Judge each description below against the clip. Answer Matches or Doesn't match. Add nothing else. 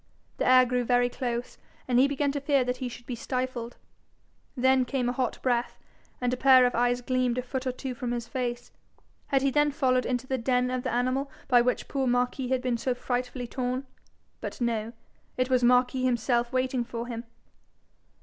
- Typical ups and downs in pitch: Doesn't match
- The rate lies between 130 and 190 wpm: Doesn't match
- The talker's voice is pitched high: Matches